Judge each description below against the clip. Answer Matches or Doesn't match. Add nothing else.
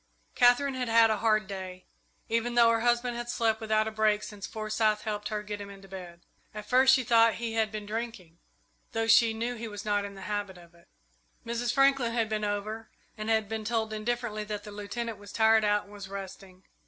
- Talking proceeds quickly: Matches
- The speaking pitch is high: Matches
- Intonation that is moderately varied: Doesn't match